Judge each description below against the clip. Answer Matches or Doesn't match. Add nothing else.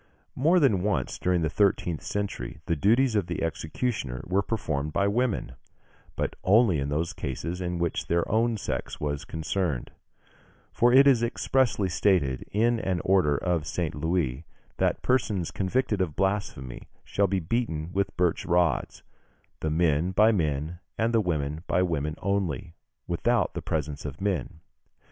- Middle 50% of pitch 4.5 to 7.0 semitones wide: Matches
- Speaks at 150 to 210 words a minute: Matches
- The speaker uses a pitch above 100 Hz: Doesn't match